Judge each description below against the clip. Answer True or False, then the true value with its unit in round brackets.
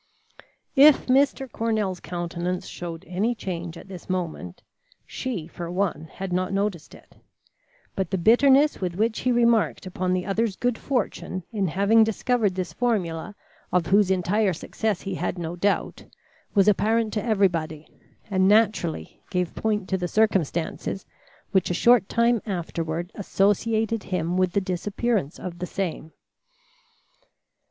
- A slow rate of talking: False (145 wpm)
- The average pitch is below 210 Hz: True (190 Hz)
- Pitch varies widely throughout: False (3.9 semitones)